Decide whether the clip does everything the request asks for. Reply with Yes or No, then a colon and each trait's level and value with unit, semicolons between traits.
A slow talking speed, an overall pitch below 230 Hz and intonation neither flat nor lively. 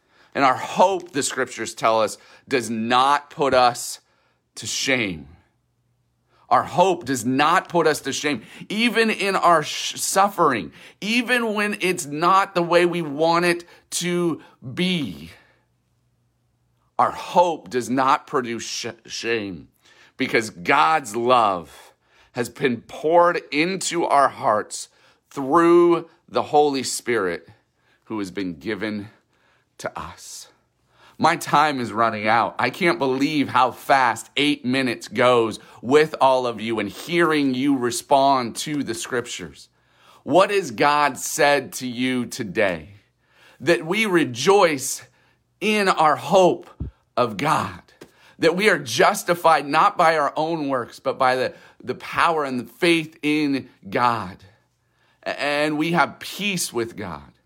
No: slow, 130 wpm; medium, 140 Hz; wide, 6.0 semitones